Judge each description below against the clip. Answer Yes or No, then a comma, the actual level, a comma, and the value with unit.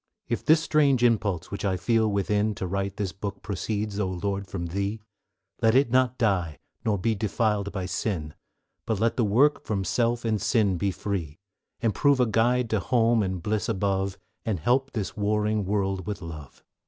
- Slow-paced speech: No, average, 190 wpm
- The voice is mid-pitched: No, low, 105 Hz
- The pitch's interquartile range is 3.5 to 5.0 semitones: No, average, 2.9 semitones